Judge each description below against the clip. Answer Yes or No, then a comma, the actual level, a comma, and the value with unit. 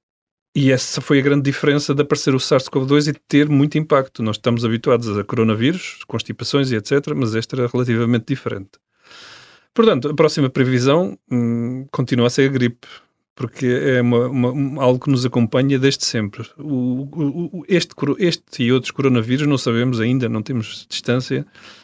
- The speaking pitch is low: Yes, low, 130 Hz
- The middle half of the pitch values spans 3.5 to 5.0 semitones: No, average, 2.9 semitones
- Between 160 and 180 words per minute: Yes, average, 170 wpm